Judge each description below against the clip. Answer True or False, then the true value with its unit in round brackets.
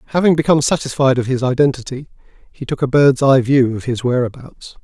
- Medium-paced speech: True (185 wpm)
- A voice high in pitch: False (130 Hz)